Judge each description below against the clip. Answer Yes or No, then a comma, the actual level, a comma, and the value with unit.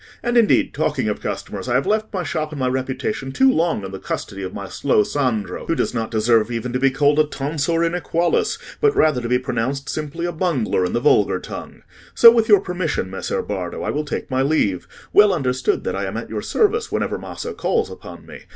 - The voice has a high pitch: No, medium, 140 Hz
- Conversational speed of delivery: No, fast, 220 wpm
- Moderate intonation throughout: No, wide, 6.6 semitones